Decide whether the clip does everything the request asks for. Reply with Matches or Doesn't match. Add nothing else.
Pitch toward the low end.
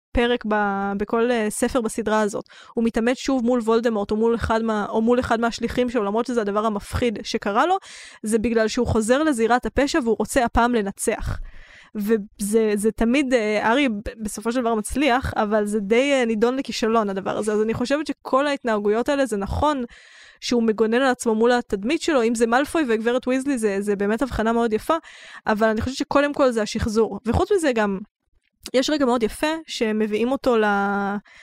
Doesn't match